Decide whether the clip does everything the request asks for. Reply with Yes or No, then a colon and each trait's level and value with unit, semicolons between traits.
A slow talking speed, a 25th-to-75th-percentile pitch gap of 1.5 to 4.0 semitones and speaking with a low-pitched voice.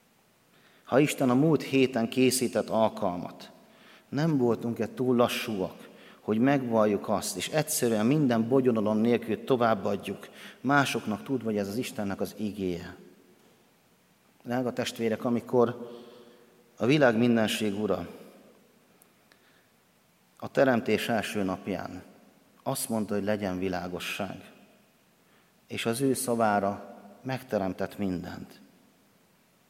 Yes: slow, 100 wpm; average, 3.1 semitones; low, 115 Hz